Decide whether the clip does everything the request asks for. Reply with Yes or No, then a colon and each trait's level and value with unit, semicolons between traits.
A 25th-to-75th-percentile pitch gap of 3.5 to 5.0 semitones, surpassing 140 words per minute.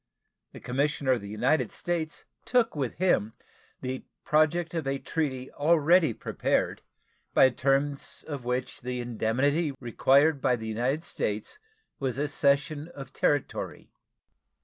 No: average, 3.8 semitones; slow, 135 wpm